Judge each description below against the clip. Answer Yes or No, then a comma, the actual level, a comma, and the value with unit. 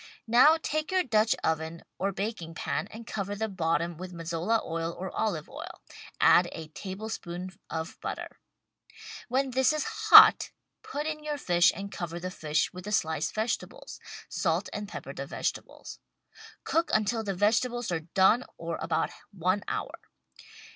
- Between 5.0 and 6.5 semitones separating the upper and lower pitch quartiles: Yes, average, 5.3 semitones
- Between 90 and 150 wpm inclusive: No, average, 160 wpm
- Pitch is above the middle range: Yes, high, 195 Hz